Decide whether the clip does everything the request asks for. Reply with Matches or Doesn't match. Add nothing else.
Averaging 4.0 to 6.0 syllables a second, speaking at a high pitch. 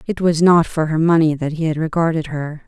Doesn't match